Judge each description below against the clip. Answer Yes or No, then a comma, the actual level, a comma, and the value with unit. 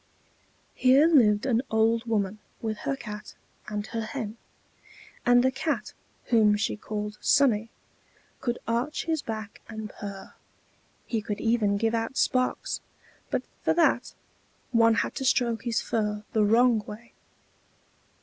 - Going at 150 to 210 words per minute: No, average, 140 wpm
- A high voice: Yes, high, 225 Hz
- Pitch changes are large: No, narrow, 2.5 semitones